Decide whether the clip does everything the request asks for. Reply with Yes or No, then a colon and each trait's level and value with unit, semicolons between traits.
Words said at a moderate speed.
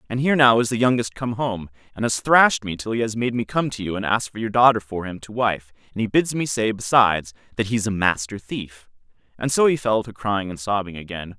No: fast, 260 wpm